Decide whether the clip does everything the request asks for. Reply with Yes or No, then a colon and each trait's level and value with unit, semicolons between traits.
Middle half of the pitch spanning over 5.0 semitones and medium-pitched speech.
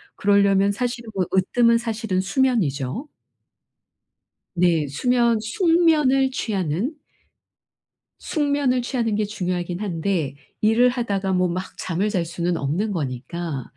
No: wide, 5.6 semitones; high, 200 Hz